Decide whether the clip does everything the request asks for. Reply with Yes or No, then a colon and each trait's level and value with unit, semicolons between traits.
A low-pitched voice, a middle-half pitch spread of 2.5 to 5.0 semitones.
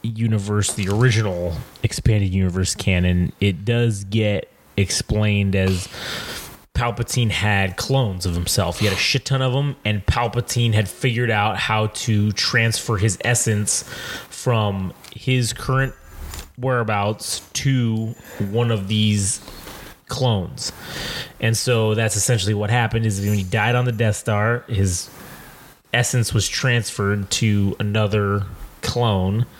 Yes: low, 110 Hz; average, 3.0 semitones